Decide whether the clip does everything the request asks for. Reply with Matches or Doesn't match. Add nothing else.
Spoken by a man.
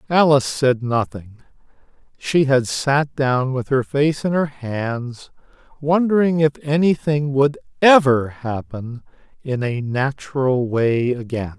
Matches